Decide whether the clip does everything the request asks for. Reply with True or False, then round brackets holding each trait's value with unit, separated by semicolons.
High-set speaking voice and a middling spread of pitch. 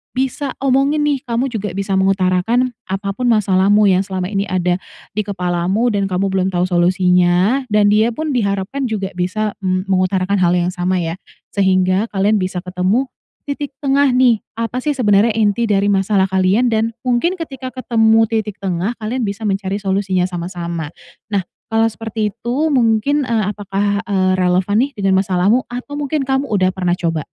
True (200 Hz; 4.0 semitones)